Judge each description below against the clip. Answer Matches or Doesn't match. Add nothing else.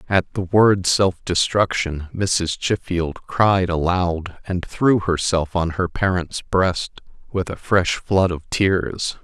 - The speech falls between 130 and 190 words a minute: Matches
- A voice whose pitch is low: Matches